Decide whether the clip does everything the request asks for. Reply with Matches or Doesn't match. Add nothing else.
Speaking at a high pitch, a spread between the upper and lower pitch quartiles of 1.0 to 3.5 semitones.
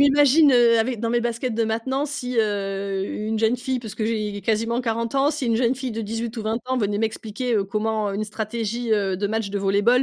Matches